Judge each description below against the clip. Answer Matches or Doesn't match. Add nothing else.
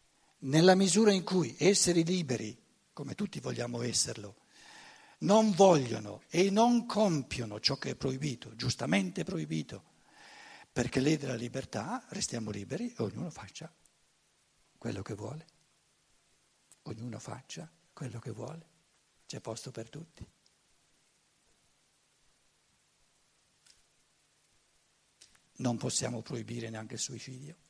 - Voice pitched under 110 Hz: Doesn't match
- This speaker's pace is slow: Matches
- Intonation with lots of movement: Matches